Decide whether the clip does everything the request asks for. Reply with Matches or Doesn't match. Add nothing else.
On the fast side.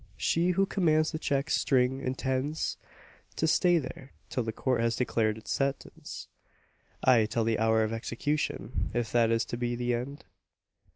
Doesn't match